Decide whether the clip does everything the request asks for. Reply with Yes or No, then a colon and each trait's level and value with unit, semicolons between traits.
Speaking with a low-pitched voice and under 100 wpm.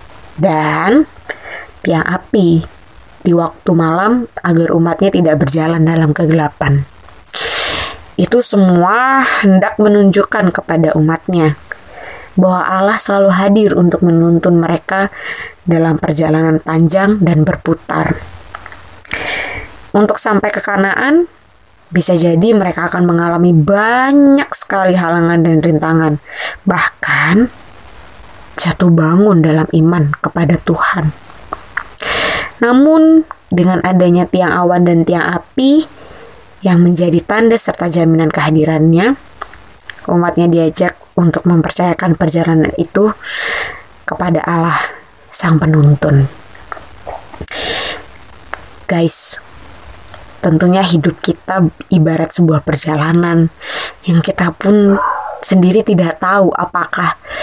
No: medium, 170 Hz; average, 90 wpm